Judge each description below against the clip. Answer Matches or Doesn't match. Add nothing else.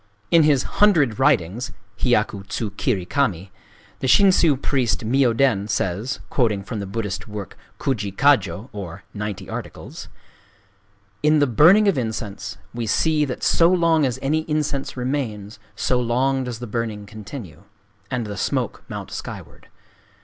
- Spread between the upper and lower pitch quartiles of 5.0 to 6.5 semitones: Matches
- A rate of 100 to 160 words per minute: Matches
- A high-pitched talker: Doesn't match